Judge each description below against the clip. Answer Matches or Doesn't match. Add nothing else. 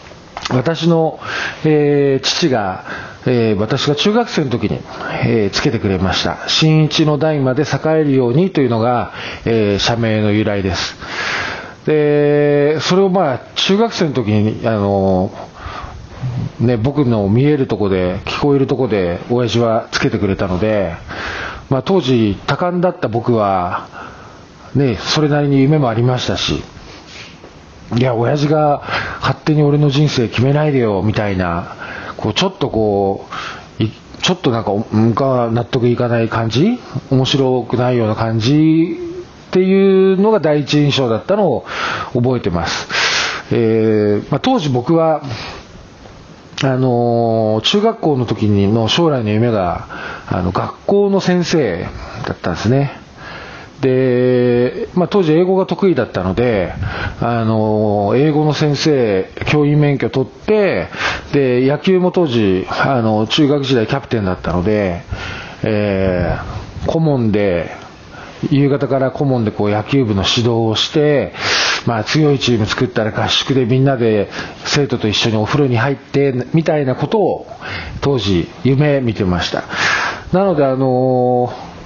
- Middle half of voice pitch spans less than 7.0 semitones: Matches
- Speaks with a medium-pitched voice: Doesn't match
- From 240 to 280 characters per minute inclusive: Matches